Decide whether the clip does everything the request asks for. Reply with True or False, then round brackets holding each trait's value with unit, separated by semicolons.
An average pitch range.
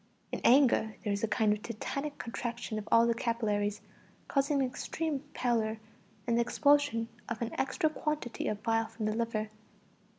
True (3.7 semitones)